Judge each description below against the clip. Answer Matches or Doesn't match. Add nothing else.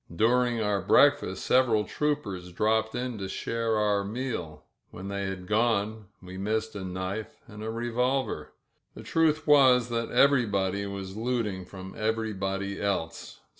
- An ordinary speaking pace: Matches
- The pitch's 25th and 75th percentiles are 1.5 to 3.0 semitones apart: Doesn't match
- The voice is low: Matches